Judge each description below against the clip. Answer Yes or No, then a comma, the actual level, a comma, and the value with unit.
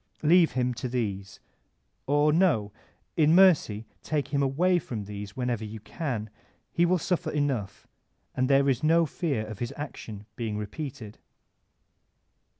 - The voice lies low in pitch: Yes, low, 130 Hz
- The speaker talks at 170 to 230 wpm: No, average, 150 wpm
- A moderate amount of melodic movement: No, wide, 6.3 semitones